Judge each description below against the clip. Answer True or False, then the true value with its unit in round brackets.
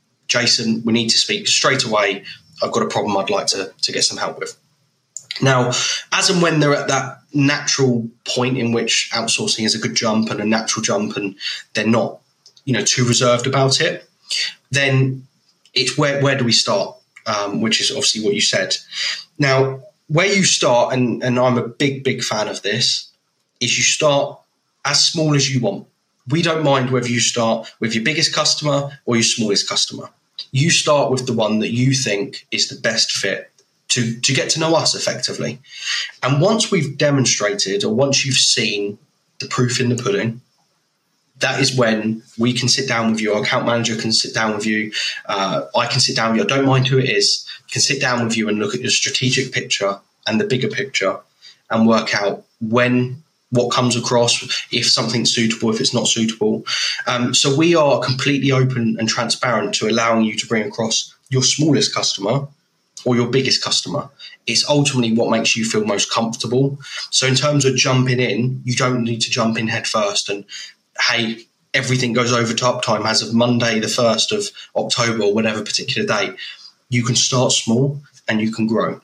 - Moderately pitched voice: False (125 Hz)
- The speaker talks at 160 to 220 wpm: True (195 wpm)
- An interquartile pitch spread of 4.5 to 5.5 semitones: False (3.2 semitones)